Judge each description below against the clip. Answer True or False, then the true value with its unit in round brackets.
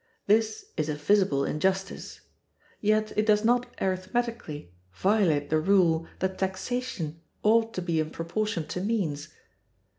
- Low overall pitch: False (190 Hz)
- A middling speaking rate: False (130 wpm)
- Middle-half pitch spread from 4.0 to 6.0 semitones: True (5.1 semitones)